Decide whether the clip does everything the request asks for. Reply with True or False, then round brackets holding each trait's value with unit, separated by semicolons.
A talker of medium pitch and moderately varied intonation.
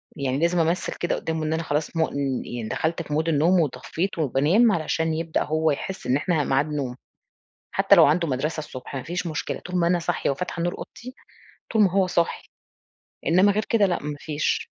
True (160 Hz; 3.1 semitones)